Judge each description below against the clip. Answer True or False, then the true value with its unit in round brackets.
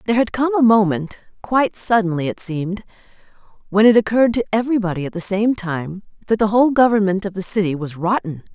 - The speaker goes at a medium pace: True (175 wpm)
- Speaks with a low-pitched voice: False (205 Hz)